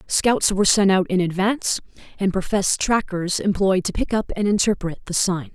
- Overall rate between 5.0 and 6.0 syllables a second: Yes, 5.3 syllables/s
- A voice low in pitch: No, high, 195 Hz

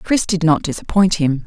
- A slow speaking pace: No, fast, 205 wpm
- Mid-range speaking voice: Yes, medium, 175 Hz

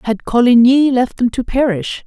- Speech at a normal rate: Yes, average, 175 wpm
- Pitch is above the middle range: Yes, high, 240 Hz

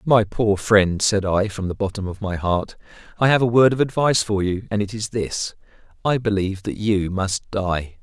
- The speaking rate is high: Yes, fast, 215 wpm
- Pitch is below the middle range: Yes, low, 100 Hz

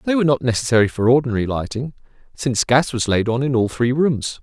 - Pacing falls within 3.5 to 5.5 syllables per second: No, 6.4 syllables/s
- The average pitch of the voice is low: Yes, low, 125 Hz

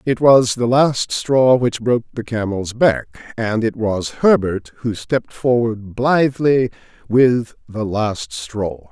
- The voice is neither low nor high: No, low, 115 Hz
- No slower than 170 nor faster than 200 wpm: No, average, 150 wpm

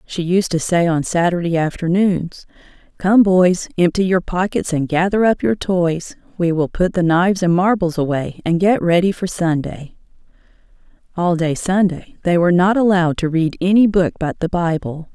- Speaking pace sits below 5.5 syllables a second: Yes, 4.9 syllables/s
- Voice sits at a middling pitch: Yes, medium, 175 Hz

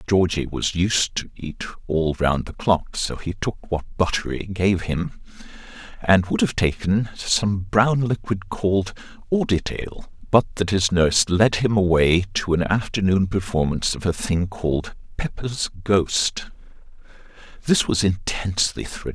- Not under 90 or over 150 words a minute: Yes, average, 145 wpm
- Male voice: Yes, male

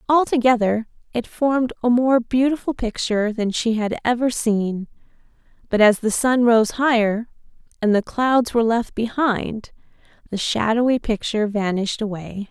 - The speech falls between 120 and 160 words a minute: Yes, average, 140 wpm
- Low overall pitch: No, high, 230 Hz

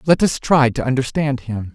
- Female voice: No, male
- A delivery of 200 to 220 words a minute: Yes, fast, 205 wpm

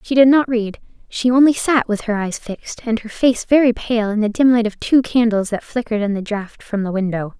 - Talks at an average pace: No, fast, 250 wpm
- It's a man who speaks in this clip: No, female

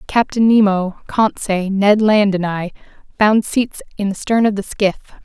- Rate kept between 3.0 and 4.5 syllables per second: Yes, 4.2 syllables/s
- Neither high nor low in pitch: No, high, 205 Hz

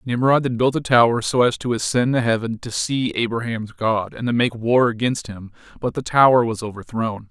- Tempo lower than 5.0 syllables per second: No, 5.1 syllables/s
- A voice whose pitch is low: Yes, low, 120 Hz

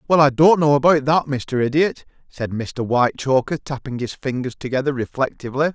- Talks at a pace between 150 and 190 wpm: Yes, average, 165 wpm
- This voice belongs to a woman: No, male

